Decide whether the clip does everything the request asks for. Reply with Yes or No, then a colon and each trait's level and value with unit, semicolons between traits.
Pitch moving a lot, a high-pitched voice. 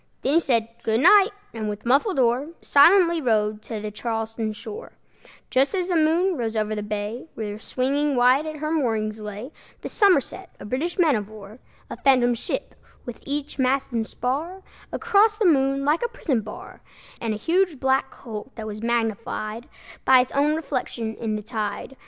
Yes: wide, 5.8 semitones; very high, 255 Hz